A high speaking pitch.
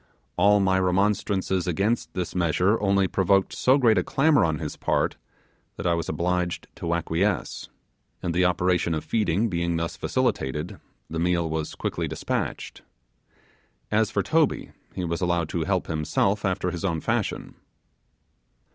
No: very low, 90 Hz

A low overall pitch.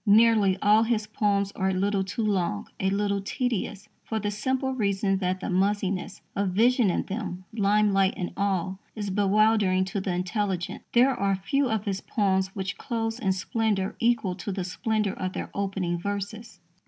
No: high, 200 Hz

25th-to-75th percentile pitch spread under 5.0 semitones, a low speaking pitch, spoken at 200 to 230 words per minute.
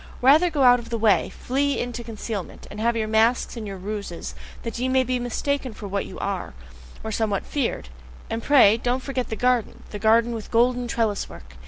No: average, 2.8 semitones; high, 230 Hz; fast, 205 wpm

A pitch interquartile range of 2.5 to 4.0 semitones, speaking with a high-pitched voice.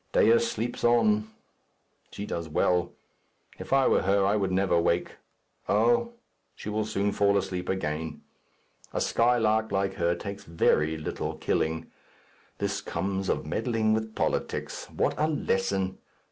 No: average, 3.2 semitones; low, 100 Hz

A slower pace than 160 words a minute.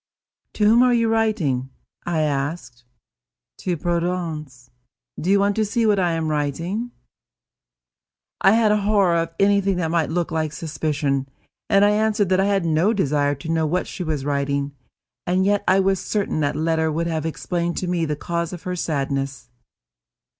No: average, 175 wpm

